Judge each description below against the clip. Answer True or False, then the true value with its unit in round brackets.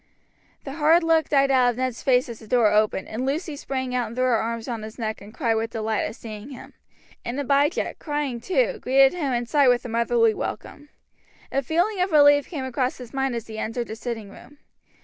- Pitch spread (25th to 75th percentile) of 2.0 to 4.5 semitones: True (4.0 semitones)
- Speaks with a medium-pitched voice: False (250 Hz)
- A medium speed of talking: False (220 wpm)